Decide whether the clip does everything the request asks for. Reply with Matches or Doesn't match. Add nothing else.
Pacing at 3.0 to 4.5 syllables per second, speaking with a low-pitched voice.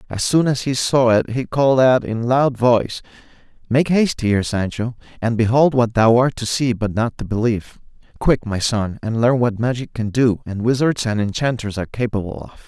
Doesn't match